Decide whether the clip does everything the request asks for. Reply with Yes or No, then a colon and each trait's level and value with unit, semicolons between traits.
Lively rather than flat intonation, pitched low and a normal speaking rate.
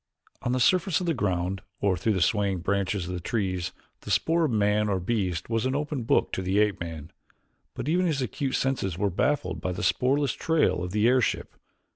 No: wide, 6.1 semitones; low, 105 Hz; fast, 210 wpm